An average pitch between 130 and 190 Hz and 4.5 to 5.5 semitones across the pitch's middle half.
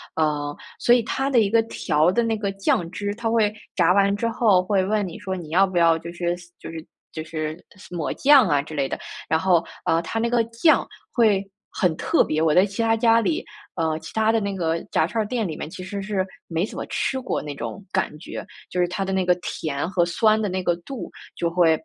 Yes: medium, 185 Hz; average, 5.0 semitones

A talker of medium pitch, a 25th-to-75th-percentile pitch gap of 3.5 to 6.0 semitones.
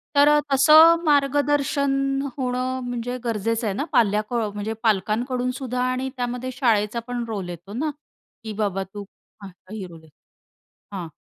No: high, 245 Hz; average, 4.3 semitones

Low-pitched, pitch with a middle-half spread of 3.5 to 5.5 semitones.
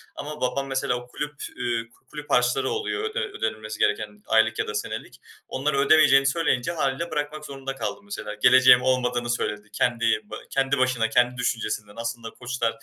No: low, 125 Hz; average, 3.1 semitones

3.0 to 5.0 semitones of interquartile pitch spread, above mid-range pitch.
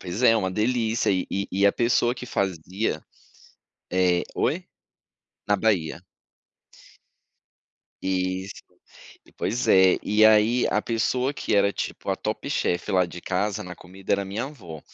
No: average, 3.4 semitones; low, 100 Hz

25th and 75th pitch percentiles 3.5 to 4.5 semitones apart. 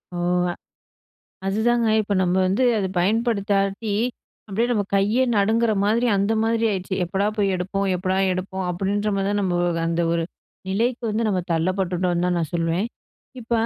No: average, 3.0 semitones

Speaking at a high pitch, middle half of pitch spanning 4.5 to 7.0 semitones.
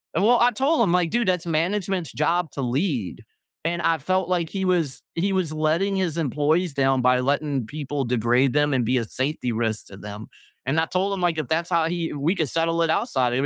No: medium, 160 Hz; average, 5.2 semitones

